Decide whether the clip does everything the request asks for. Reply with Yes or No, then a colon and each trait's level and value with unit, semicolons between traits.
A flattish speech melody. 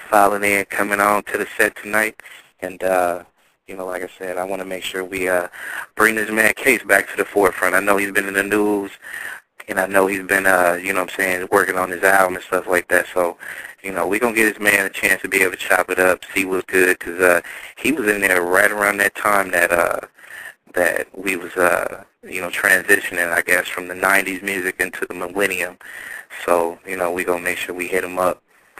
Yes: narrow, 1.6 semitones